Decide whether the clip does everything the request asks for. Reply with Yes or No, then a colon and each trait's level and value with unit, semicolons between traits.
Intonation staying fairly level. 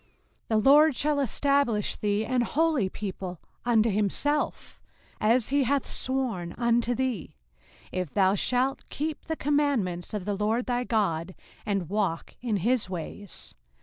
No: average, 5.1 semitones